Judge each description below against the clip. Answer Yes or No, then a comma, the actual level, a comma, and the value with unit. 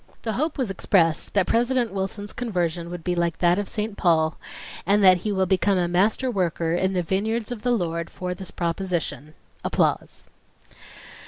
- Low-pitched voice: No, high, 190 Hz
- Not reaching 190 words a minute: Yes, average, 175 wpm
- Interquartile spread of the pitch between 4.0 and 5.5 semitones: No, average, 3.5 semitones